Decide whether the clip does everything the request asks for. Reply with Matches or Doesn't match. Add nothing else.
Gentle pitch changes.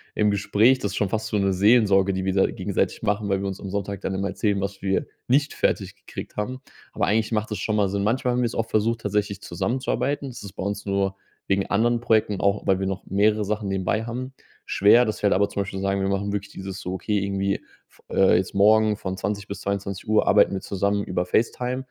Matches